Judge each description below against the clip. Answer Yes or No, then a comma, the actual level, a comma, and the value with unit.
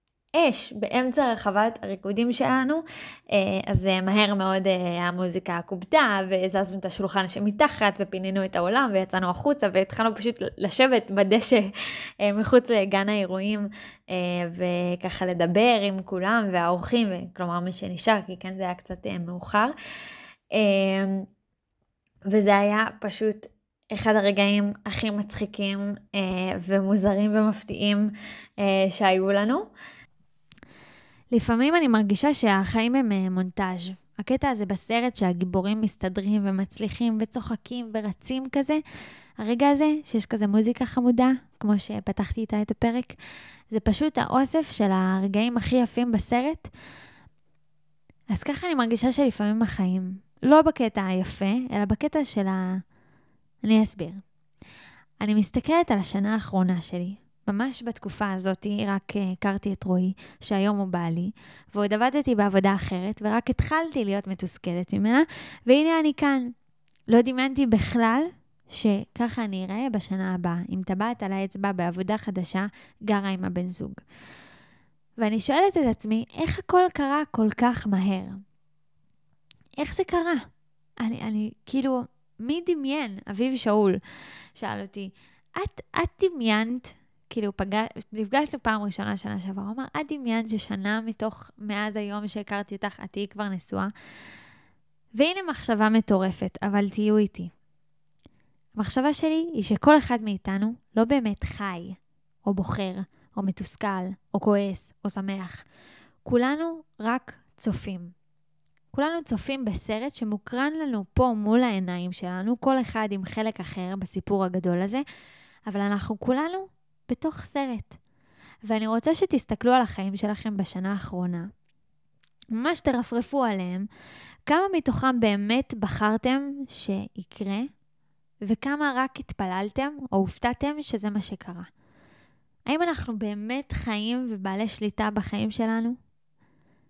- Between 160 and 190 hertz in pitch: No, high, 210 Hz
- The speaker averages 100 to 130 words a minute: Yes, average, 120 wpm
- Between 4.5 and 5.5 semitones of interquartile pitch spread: No, average, 4.0 semitones